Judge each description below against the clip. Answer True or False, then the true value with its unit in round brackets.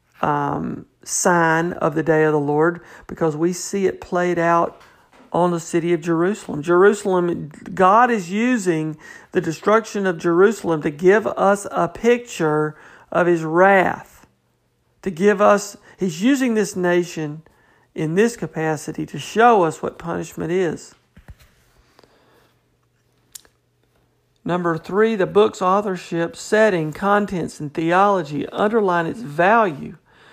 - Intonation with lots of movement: False (3.8 semitones)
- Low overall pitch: False (175 Hz)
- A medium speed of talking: False (125 wpm)